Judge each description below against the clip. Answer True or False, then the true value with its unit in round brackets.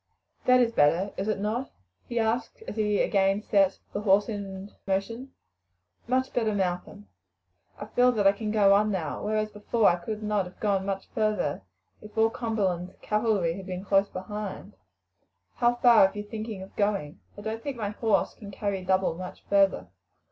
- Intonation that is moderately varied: False (2.3 semitones)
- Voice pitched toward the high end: True (205 Hz)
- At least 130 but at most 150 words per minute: False (180 wpm)